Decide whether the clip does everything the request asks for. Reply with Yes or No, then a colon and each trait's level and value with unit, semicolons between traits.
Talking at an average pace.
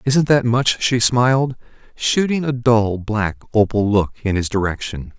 Yes: average, 160 wpm